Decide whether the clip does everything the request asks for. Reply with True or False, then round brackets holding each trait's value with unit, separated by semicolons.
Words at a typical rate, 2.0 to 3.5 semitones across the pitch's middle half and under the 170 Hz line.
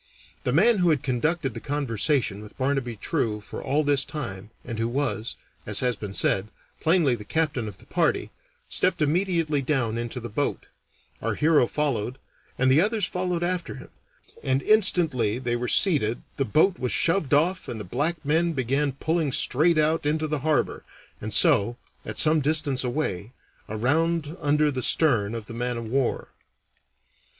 False (170 wpm; 5.0 semitones; 140 Hz)